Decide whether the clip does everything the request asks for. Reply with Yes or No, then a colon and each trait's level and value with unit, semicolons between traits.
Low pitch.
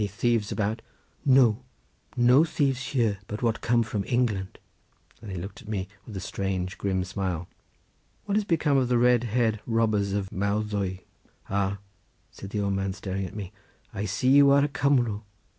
Yes: low, 105 Hz